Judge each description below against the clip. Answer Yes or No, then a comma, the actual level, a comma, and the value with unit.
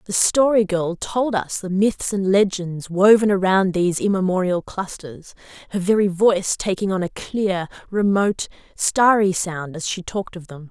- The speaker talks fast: No, average, 165 wpm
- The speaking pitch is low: No, high, 190 Hz